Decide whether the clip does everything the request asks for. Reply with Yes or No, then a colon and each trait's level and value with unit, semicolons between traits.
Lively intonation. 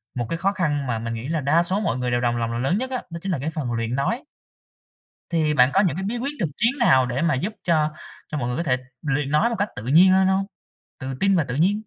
Yes: wide, 7.0 semitones